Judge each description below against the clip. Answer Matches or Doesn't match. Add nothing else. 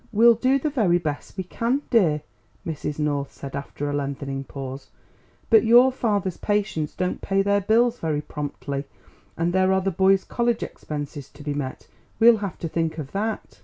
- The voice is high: Doesn't match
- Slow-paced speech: Doesn't match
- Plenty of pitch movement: Matches